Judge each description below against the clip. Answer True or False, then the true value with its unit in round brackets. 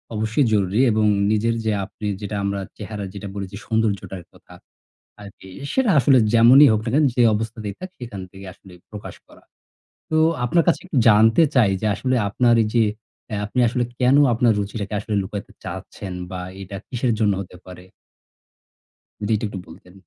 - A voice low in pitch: True (110 Hz)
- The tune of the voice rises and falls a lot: False (3.3 semitones)